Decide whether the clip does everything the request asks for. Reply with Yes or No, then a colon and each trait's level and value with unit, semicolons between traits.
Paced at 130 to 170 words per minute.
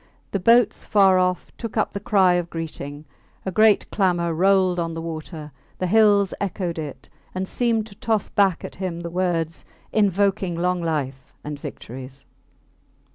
Yes: average, 160 wpm